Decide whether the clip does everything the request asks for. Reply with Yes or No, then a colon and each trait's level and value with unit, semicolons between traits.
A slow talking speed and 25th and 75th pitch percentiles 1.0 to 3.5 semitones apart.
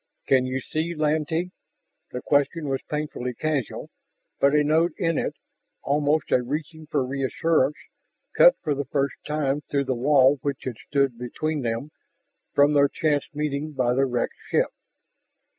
No: average, 155 wpm; narrow, 2.4 semitones